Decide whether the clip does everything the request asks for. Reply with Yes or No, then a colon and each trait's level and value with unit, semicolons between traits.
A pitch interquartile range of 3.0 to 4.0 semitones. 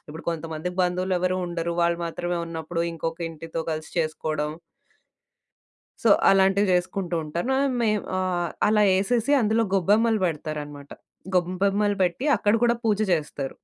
Yes: average, 3.3 semitones